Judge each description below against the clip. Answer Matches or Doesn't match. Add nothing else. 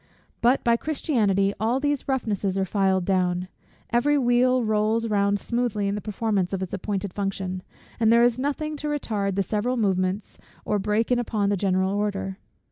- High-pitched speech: Matches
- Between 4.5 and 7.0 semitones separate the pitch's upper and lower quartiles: Doesn't match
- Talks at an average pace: Matches